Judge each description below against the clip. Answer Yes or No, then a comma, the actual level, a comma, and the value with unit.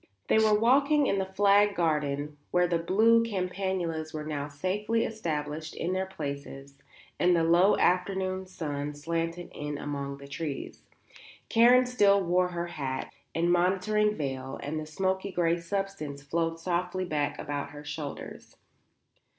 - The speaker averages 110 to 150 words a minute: Yes, average, 145 wpm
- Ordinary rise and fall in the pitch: Yes, average, 4.5 semitones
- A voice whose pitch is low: No, medium, 175 Hz